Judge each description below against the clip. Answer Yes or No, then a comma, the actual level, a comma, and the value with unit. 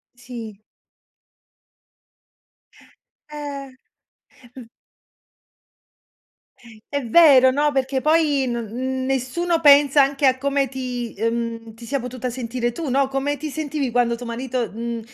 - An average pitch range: Yes, average, 3.0 semitones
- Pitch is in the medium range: No, very high, 260 Hz